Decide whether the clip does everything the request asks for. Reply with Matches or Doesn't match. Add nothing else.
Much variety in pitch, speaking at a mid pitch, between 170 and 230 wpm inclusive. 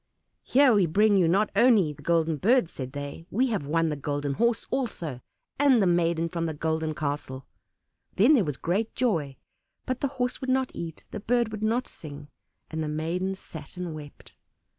Matches